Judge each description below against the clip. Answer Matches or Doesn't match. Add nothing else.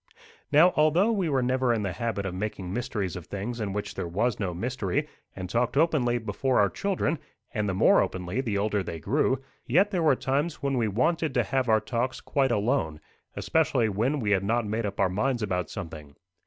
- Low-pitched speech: Matches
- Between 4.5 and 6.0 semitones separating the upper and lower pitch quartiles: Matches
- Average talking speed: Doesn't match